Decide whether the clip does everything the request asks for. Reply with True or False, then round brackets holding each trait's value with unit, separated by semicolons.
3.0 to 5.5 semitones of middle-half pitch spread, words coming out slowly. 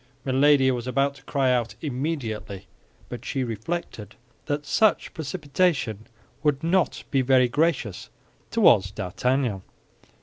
True (3.8 semitones; 115 wpm)